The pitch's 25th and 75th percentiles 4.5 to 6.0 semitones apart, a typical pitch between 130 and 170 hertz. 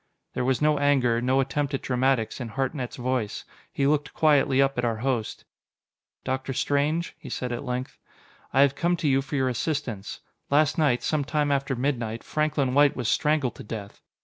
No: average, 2.7 semitones; low, 135 Hz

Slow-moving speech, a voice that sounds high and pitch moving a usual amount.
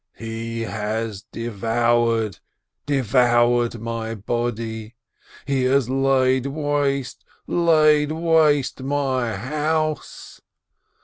No: slow, 75 wpm; low, 120 Hz; average, 3.8 semitones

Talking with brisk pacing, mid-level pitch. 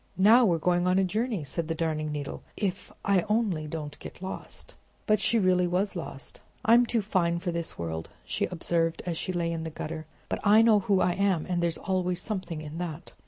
Yes: fast, 210 wpm; medium, 180 Hz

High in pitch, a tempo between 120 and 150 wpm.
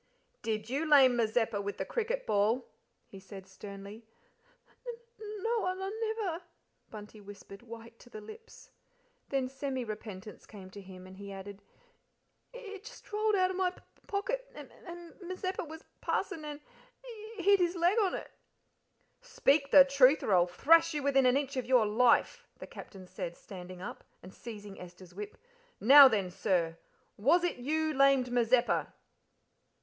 No: very high, 260 Hz; average, 170 wpm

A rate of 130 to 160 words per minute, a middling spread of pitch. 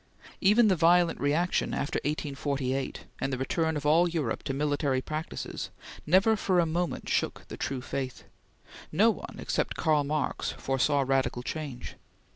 Yes: average, 150 wpm; average, 3.9 semitones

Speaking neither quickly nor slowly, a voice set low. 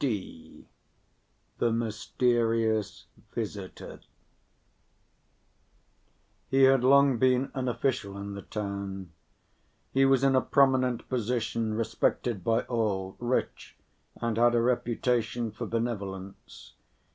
No: slow, 100 wpm; low, 115 Hz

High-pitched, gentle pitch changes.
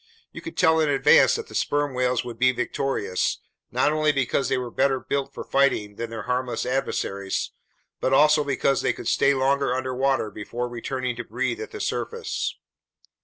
No: low, 130 Hz; narrow, 2.3 semitones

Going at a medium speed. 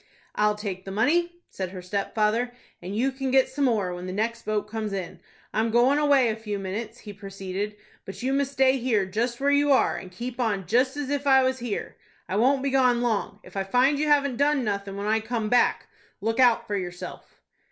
No: fast, 220 wpm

